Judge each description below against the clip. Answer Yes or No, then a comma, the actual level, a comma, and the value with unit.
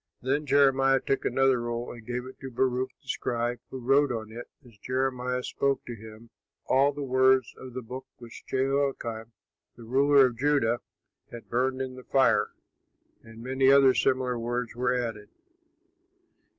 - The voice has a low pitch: Yes, low, 130 Hz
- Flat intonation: Yes, narrow, 2.1 semitones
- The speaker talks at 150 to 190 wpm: Yes, average, 165 wpm